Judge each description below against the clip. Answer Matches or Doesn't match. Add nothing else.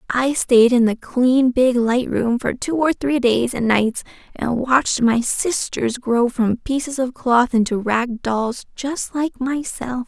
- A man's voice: Doesn't match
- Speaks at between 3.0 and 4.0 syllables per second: Matches